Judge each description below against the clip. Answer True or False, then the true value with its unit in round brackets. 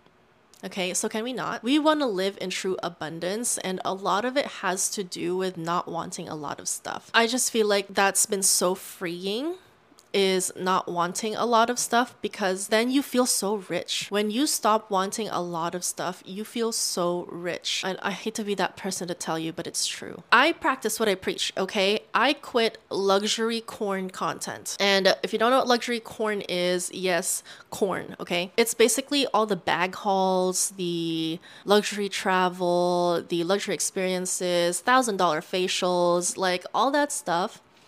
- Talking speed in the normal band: True (180 wpm)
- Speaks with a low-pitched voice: False (195 Hz)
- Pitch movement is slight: False (3.7 semitones)